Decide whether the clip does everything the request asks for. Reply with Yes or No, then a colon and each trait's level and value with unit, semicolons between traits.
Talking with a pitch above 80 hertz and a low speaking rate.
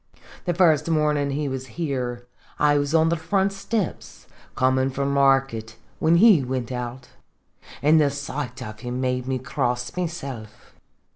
No: medium, 140 Hz; average, 150 wpm